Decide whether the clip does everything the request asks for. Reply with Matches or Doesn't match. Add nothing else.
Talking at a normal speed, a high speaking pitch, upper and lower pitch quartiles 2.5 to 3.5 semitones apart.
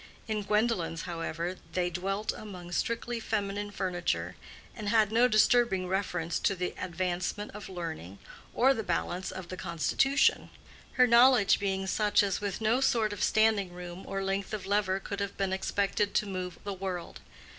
Matches